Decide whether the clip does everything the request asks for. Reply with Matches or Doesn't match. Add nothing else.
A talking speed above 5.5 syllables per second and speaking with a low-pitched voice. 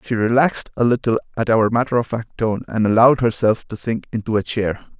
Matches